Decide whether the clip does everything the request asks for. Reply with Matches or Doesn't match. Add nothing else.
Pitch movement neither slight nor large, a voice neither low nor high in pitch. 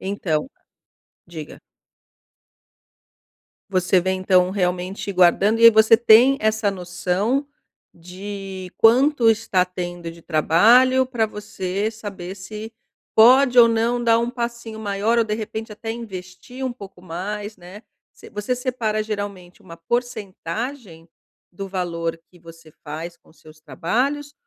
Doesn't match